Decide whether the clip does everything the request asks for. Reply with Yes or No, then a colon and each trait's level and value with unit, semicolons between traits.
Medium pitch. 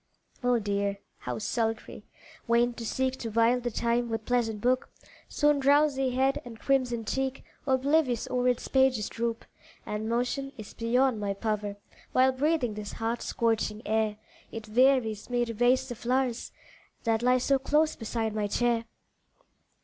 No: high, 240 Hz